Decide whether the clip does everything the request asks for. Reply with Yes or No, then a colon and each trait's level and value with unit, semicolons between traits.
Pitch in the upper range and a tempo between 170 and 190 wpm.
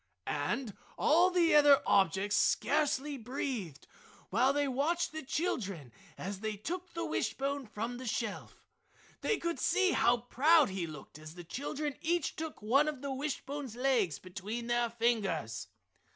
No: very high, 250 Hz; average, 150 wpm